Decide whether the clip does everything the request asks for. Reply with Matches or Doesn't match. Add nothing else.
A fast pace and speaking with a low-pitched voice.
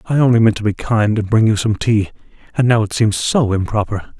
Matches